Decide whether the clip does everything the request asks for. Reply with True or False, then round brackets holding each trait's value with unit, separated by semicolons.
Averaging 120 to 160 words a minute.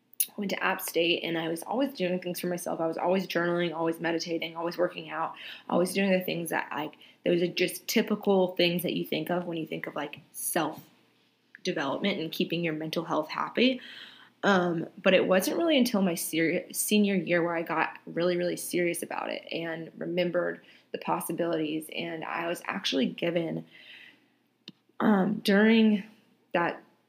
False (175 wpm)